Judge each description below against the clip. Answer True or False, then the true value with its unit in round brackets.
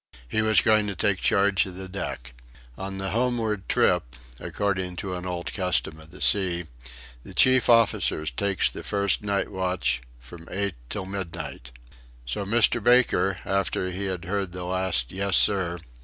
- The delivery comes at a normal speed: True (165 wpm)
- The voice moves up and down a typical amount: False (2.2 semitones)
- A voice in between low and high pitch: False (95 Hz)